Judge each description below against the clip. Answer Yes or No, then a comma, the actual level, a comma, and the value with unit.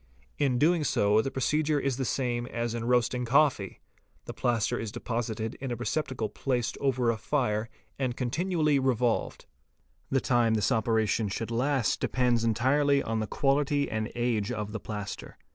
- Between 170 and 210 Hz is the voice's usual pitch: No, low, 120 Hz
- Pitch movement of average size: Yes, average, 3.4 semitones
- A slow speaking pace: No, average, 165 wpm